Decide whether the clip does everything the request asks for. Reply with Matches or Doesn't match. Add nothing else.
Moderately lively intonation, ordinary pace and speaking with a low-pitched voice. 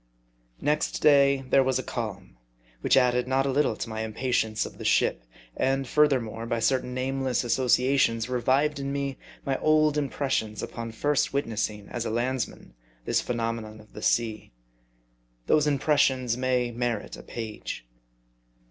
Matches